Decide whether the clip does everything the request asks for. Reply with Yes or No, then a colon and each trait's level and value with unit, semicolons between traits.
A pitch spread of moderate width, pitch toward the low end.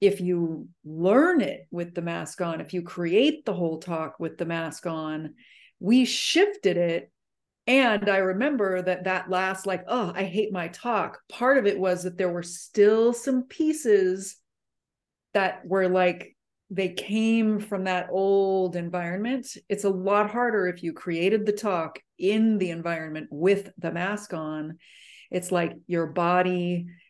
No: average, 3.2 semitones; medium, 185 Hz